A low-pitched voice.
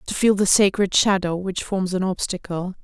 No: high, 190 Hz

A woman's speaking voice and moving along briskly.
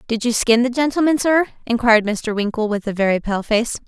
Yes: female; fast, 215 wpm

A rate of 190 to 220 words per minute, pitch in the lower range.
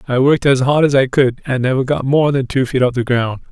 No: fast, 290 wpm; low, 130 Hz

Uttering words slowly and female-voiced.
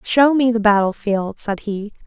No: fast, 205 wpm; female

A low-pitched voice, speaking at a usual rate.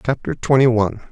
Yes: low, 120 Hz; average, 160 wpm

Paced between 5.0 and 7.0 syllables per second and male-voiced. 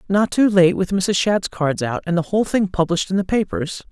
No: 5.5 syllables/s; female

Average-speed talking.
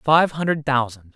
Yes: average, 155 wpm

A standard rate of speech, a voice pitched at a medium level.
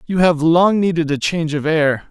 No: fast, 230 wpm; medium, 165 Hz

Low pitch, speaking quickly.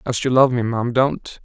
Yes: low, 125 Hz; fast, 250 wpm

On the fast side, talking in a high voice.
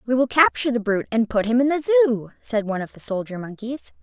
Yes: fast, 255 wpm; high, 235 Hz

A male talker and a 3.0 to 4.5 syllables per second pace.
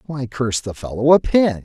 No: male; 5.4 syllables/s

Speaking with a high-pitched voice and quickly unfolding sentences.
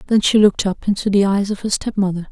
Yes: high, 200 Hz; fast, 285 wpm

